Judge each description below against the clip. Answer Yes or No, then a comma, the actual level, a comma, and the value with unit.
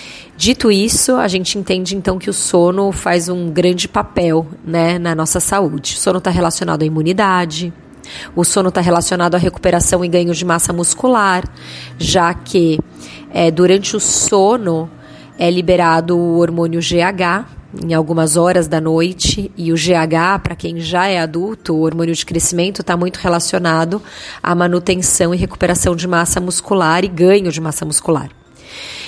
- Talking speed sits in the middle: Yes, average, 160 wpm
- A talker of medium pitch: Yes, medium, 175 Hz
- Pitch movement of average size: No, narrow, 2.0 semitones